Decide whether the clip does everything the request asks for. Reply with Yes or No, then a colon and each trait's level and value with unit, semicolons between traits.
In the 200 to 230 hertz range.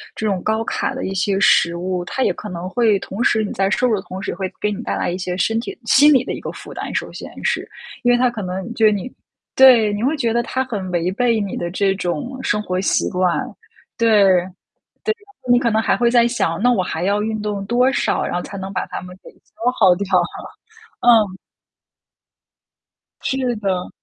Yes: high, 210 Hz